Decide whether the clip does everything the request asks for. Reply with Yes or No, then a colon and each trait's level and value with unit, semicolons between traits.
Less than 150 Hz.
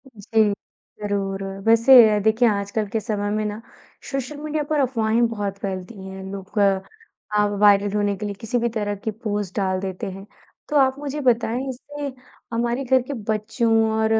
No: high, 220 Hz